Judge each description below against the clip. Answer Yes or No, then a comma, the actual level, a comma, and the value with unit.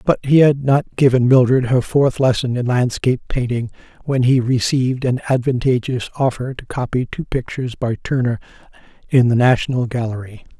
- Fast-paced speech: No, average, 160 wpm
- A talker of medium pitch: No, low, 125 Hz